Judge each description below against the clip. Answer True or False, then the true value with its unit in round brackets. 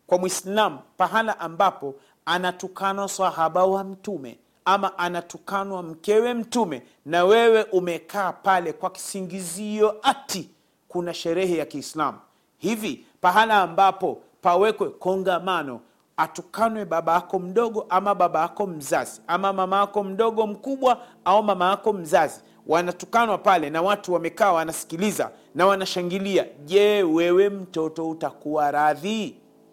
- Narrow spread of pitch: False (3.1 semitones)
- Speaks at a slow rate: False (115 wpm)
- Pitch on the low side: False (190 Hz)